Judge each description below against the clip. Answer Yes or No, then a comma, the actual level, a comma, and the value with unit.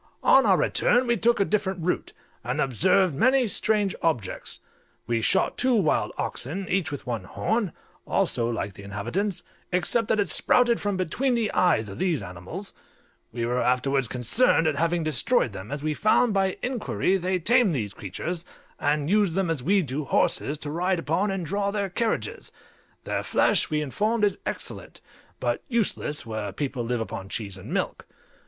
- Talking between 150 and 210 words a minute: Yes, average, 175 wpm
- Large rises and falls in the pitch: Yes, wide, 8.4 semitones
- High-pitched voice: No, medium, 170 Hz